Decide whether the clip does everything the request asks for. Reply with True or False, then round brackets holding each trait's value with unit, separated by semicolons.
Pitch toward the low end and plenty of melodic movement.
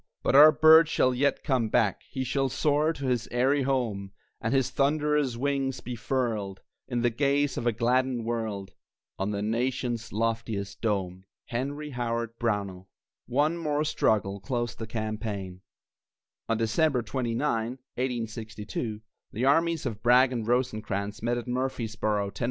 False (120 Hz; 3.5 semitones)